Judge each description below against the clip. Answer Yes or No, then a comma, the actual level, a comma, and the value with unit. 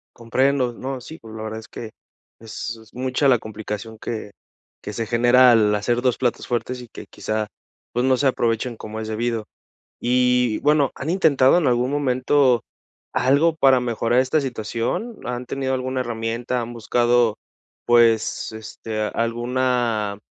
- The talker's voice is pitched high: No, low, 120 Hz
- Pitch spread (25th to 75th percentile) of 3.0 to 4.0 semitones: No, narrow, 2.4 semitones